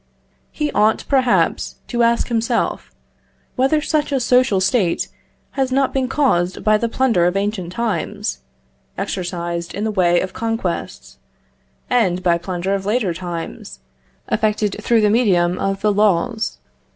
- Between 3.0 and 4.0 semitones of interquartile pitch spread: No, average, 5.1 semitones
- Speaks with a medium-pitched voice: No, high, 210 Hz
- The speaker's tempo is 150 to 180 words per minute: No, average, 140 wpm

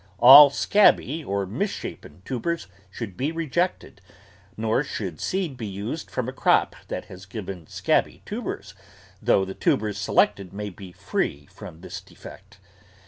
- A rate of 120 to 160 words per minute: Yes, average, 140 wpm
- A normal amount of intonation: No, wide, 6.7 semitones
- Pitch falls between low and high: No, low, 110 Hz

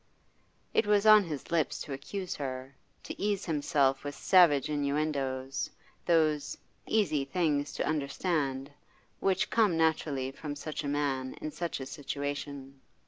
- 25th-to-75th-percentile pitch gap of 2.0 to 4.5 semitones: Yes, average, 3.4 semitones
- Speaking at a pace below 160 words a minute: Yes, average, 140 wpm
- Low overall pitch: No, medium, 145 Hz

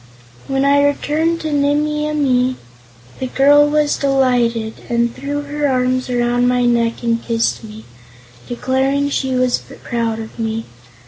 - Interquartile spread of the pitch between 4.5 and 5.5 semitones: No, average, 3.2 semitones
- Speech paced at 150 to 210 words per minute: No, average, 140 wpm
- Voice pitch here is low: No, very high, 260 Hz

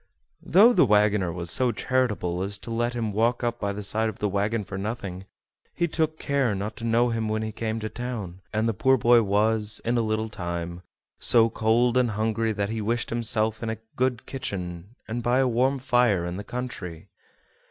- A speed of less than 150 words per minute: No, fast, 205 wpm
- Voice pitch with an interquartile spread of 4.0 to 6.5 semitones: No, average, 3.0 semitones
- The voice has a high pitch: No, low, 110 Hz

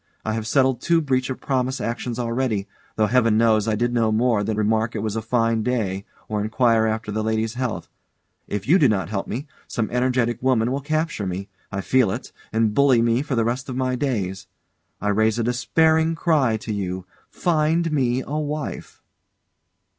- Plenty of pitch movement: No, average, 3.2 semitones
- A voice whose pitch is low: Yes, low, 115 Hz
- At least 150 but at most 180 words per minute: No, average, 190 wpm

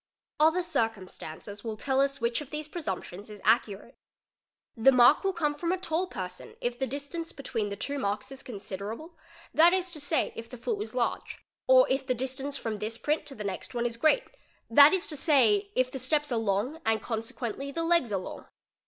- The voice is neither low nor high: No, very high, 265 Hz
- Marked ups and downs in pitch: Yes, wide, 5.7 semitones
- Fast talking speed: Yes, fast, 210 wpm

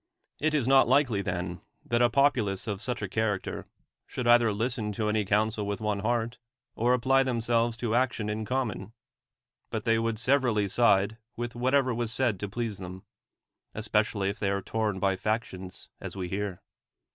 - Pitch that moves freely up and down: No, average, 2.9 semitones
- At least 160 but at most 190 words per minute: Yes, average, 180 wpm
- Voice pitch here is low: Yes, low, 110 Hz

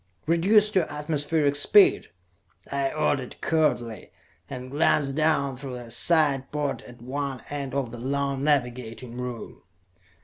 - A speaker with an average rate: No, slow, 130 wpm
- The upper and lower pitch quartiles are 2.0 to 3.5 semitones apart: Yes, average, 3.1 semitones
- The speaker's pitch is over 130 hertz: Yes, medium, 140 Hz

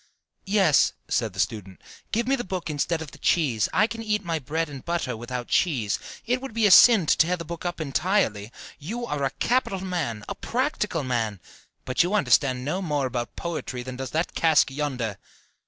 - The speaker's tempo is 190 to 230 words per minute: Yes, average, 200 wpm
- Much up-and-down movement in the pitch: Yes, wide, 7.0 semitones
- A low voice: No, medium, 155 Hz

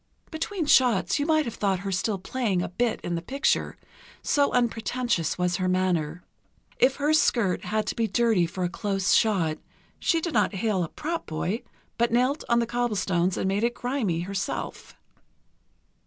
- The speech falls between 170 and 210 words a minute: Yes, average, 175 wpm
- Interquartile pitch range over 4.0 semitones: Yes, average, 5.2 semitones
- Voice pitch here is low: No, high, 215 Hz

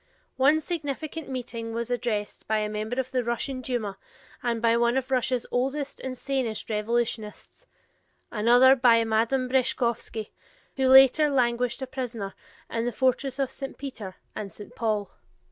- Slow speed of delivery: No, average, 150 wpm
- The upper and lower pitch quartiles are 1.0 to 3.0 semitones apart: Yes, average, 2.7 semitones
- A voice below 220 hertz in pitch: No, high, 245 Hz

